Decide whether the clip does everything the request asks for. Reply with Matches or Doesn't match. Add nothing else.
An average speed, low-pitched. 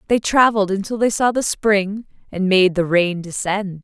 Doesn't match